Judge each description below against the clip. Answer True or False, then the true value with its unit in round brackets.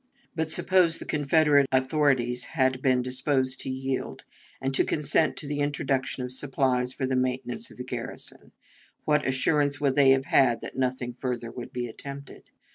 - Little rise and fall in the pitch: True (2.2 semitones)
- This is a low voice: True (130 Hz)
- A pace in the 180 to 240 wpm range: False (170 wpm)